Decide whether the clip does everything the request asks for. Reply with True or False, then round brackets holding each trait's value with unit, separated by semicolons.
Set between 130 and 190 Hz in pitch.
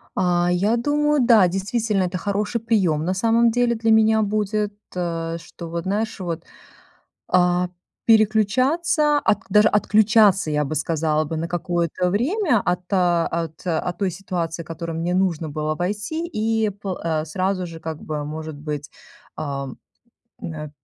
True (185 Hz)